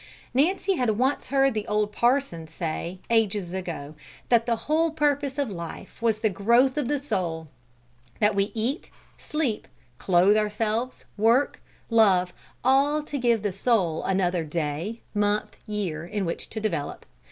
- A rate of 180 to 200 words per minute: No, average, 150 wpm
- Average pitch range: No, wide, 5.7 semitones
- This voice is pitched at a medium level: No, high, 215 Hz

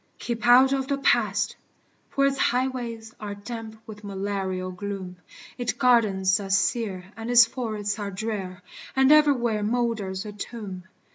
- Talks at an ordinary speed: Yes, average, 145 wpm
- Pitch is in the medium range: No, high, 220 Hz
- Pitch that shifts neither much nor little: Yes, average, 3.6 semitones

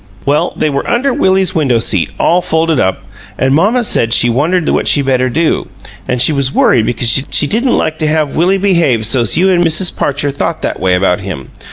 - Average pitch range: No, wide, 6.1 semitones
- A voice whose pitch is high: No, medium, 145 Hz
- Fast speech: Yes, fast, 210 wpm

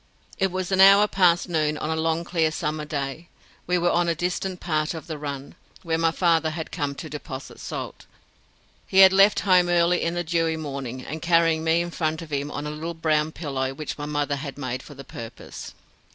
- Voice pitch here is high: No, medium, 160 Hz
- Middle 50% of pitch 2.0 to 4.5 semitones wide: Yes, average, 2.7 semitones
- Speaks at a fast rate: Yes, fast, 210 wpm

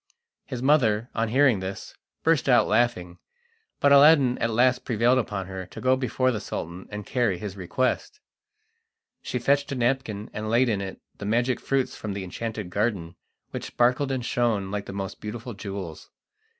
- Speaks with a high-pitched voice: No, low, 115 Hz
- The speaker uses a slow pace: No, average, 175 wpm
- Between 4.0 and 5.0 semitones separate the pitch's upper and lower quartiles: Yes, average, 4.3 semitones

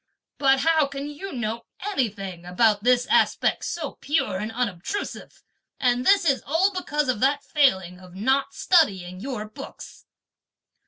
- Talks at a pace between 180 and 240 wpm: No, average, 145 wpm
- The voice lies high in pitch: Yes, very high, 255 Hz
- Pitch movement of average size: No, wide, 6.0 semitones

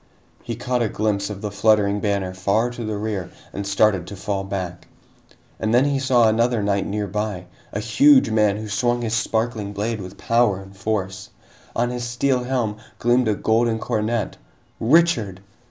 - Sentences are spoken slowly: No, average, 170 wpm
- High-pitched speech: No, low, 110 Hz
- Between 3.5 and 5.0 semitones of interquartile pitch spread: No, average, 3.0 semitones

